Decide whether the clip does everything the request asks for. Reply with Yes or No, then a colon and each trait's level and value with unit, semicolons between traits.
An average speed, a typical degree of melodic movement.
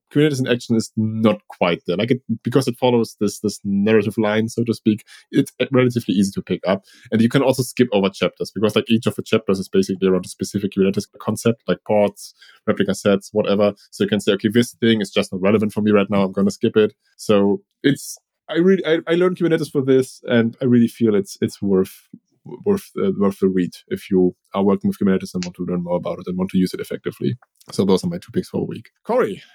No: fast, 245 wpm; average, 3.5 semitones